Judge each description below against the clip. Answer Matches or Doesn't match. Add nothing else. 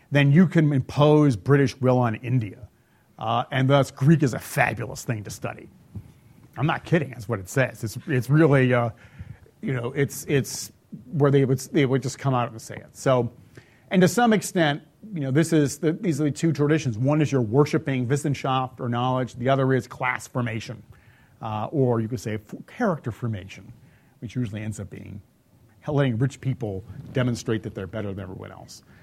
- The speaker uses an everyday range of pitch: Matches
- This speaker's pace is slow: Doesn't match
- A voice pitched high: Doesn't match